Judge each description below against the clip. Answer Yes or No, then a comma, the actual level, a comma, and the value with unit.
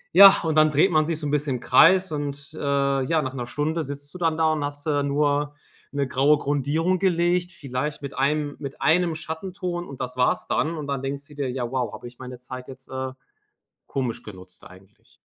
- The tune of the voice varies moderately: Yes, average, 3.2 semitones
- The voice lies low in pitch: No, medium, 145 Hz